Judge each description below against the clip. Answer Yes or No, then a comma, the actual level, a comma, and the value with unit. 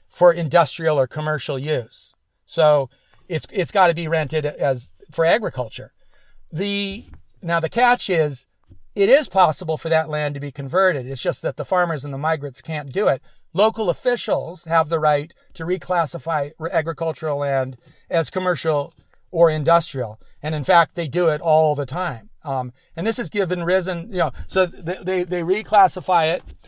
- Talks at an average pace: Yes, average, 170 wpm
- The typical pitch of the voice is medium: Yes, medium, 165 Hz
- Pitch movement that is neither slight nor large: Yes, average, 3.8 semitones